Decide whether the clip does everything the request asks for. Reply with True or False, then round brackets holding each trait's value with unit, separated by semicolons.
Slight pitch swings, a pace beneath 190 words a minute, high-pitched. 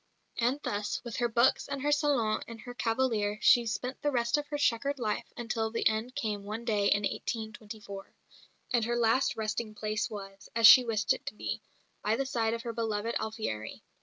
False (2.3 semitones; 195 wpm; 225 Hz)